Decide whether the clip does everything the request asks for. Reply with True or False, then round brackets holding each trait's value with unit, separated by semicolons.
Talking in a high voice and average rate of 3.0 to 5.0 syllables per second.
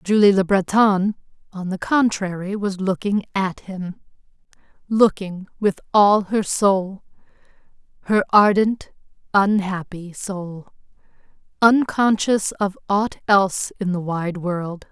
True (195 Hz; 3.7 syllables/s)